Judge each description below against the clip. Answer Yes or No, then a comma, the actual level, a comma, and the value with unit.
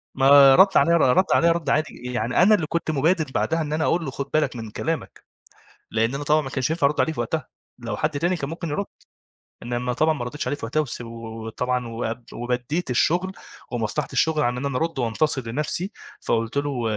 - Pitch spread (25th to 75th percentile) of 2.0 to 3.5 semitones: No, average, 4.6 semitones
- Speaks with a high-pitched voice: No, medium, 140 Hz